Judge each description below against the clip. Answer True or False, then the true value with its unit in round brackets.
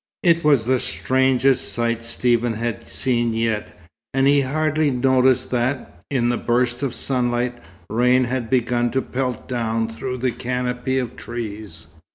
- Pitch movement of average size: False (1.8 semitones)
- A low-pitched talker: True (125 Hz)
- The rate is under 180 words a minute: True (150 wpm)